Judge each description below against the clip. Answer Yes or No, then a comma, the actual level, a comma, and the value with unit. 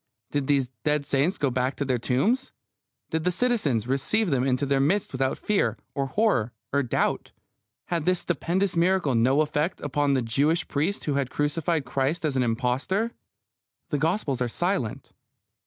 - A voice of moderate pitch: Yes, medium, 145 Hz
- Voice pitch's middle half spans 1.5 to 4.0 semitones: No, average, 4.8 semitones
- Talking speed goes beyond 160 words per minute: Yes, average, 170 wpm